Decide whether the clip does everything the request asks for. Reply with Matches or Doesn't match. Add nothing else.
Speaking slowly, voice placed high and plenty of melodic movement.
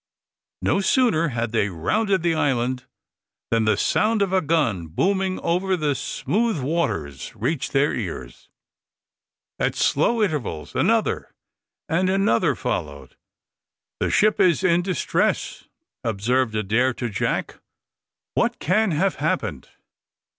Doesn't match